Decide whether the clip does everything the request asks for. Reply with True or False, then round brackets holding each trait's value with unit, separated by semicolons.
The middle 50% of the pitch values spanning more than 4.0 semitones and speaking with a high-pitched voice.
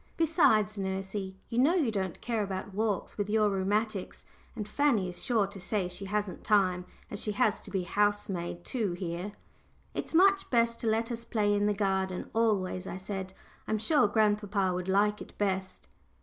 False (2.5 semitones; 205 Hz)